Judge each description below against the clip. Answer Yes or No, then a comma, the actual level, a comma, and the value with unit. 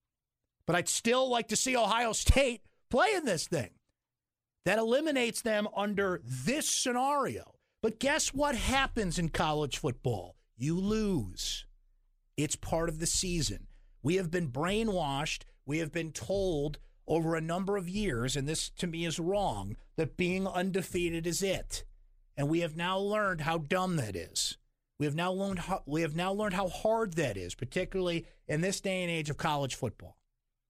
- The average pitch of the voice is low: No, medium, 175 Hz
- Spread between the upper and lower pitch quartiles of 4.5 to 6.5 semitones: Yes, wide, 5.5 semitones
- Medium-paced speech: Yes, average, 160 wpm